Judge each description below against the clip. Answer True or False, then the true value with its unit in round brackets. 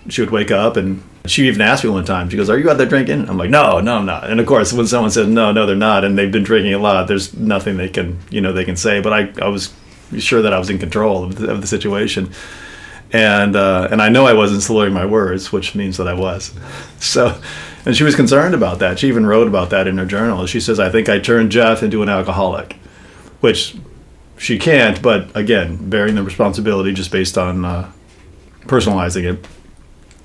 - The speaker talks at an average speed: False (235 wpm)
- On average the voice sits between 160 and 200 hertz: False (100 Hz)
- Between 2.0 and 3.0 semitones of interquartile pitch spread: True (2.7 semitones)